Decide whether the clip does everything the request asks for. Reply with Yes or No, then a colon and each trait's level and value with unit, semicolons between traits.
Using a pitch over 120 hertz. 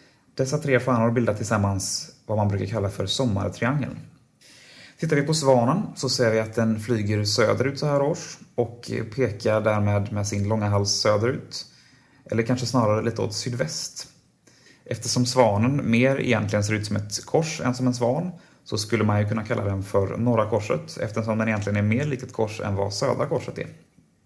No: low, 115 Hz